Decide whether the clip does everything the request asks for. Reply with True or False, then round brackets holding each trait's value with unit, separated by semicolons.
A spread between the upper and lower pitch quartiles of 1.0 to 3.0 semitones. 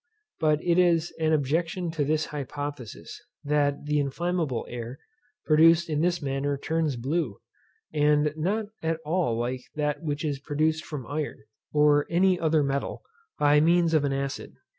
True (2.4 semitones)